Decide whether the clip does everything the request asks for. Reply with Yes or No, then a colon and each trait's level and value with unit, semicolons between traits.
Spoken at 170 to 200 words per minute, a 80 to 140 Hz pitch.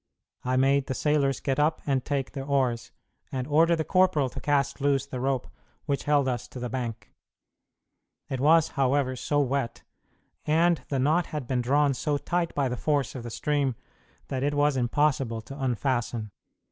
Yes: average, 180 wpm; low, 135 Hz